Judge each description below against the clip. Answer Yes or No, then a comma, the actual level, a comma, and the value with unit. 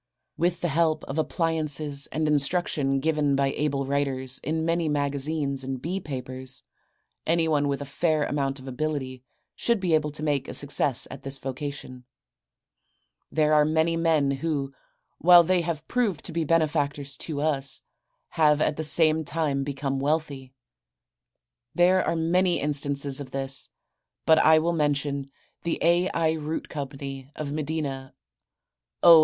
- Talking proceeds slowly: No, average, 150 wpm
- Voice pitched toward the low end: No, medium, 150 Hz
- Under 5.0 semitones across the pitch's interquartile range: Yes, average, 2.7 semitones